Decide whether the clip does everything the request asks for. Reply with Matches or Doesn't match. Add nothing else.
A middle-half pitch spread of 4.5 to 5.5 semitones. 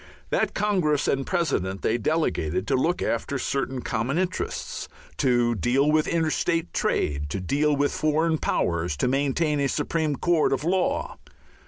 Matches